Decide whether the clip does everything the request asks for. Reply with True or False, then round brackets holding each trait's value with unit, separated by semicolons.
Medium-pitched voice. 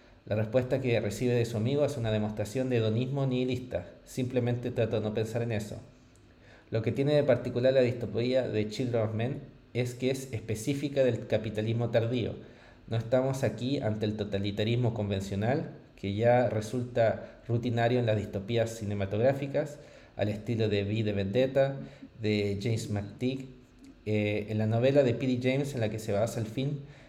False (120 Hz)